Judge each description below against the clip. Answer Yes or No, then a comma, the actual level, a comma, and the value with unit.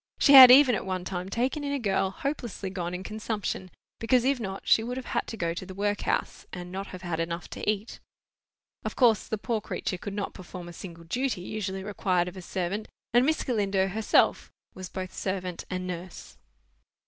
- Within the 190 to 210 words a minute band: Yes, fast, 205 wpm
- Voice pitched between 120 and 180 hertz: No, high, 195 Hz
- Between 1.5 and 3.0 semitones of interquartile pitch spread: No, average, 3.7 semitones